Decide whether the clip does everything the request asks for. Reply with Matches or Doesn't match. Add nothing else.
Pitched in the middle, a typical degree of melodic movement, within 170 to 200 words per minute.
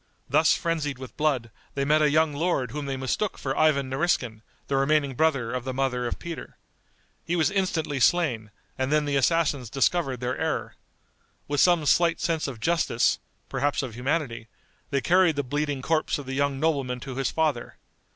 Matches